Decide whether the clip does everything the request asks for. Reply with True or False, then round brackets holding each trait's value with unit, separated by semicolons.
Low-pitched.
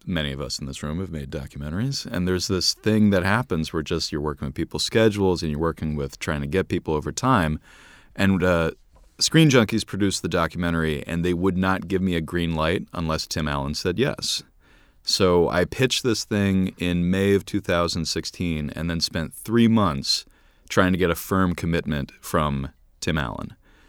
True (85 Hz)